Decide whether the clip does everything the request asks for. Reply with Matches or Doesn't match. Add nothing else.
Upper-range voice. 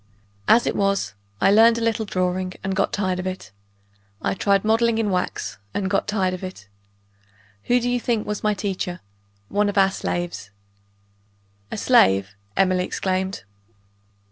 Matches